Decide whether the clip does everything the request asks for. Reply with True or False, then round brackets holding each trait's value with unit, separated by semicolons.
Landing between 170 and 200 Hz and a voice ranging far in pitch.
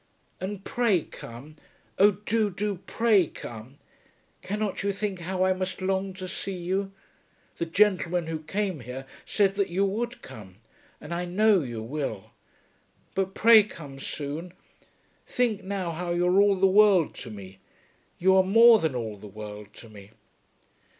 True (185 Hz; 5.7 semitones)